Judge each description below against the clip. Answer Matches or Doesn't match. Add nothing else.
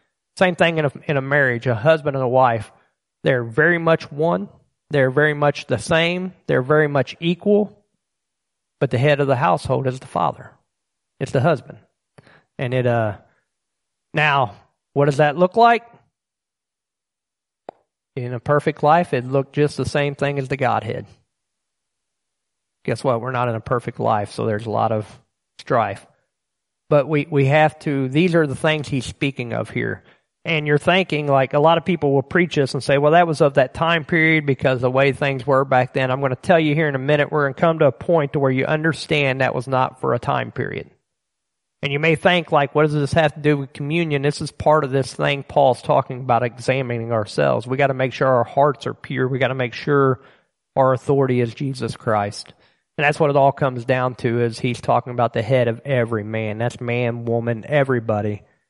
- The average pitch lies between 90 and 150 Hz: Matches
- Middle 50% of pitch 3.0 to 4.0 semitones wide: Matches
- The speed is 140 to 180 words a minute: Doesn't match